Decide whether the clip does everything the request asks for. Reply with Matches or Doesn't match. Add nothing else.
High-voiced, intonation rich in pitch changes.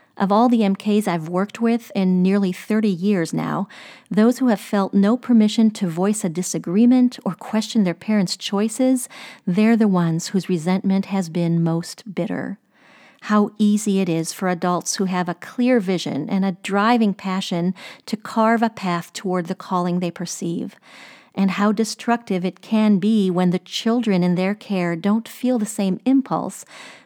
Doesn't match